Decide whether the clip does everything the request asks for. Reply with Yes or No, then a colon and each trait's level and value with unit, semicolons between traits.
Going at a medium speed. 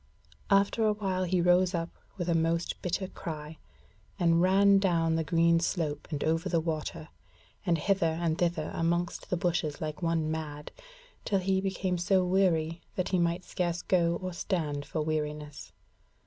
Yes: average, 165 wpm